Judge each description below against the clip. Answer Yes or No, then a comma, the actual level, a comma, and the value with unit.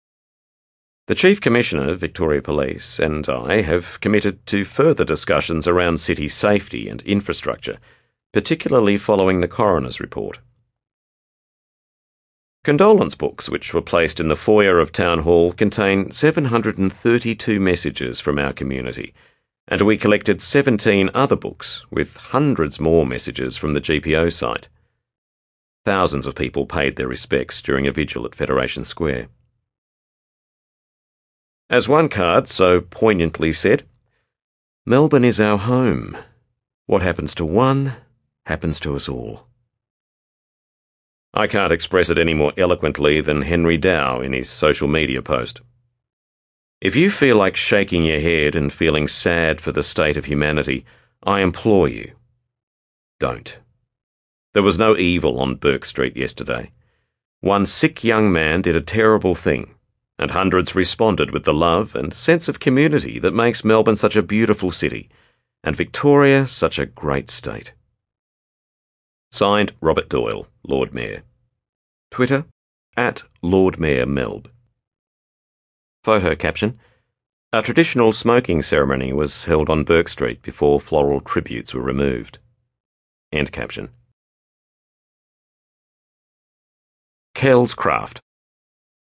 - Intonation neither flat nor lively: No, wide, 8.0 semitones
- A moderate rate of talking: No, slow, 125 wpm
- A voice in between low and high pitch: No, very low, 90 Hz